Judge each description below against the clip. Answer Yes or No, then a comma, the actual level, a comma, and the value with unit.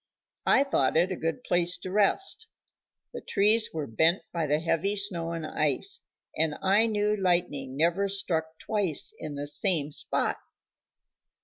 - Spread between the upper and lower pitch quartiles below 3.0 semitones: No, average, 4.2 semitones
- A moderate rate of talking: Yes, average, 150 wpm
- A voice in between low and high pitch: Yes, medium, 170 Hz